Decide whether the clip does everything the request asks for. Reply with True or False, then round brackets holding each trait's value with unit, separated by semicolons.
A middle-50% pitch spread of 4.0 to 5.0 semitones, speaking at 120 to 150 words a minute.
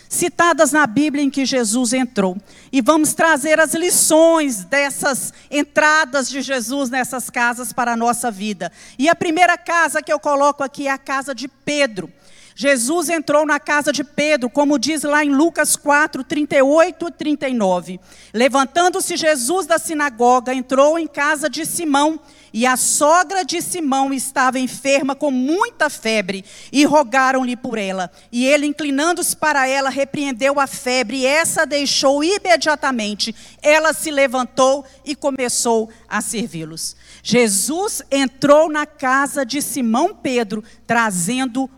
False (3.2 semitones; 145 wpm)